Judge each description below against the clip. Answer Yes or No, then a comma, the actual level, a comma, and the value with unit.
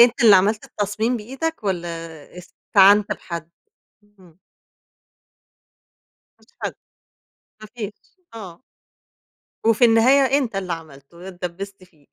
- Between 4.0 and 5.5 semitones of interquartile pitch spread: Yes, average, 4.3 semitones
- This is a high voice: Yes, high, 200 Hz